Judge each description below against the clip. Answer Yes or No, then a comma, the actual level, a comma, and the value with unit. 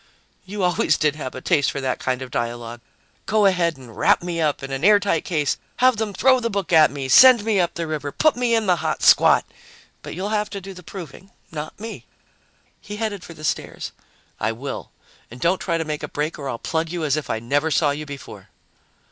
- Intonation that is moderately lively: No, wide, 5.9 semitones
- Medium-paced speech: No, fast, 230 wpm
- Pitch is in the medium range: Yes, medium, 165 Hz